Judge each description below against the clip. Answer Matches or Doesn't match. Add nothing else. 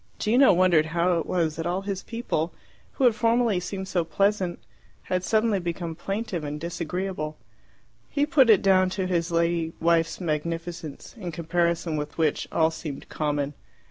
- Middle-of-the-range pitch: Matches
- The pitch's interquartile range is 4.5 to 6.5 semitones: Doesn't match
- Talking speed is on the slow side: Doesn't match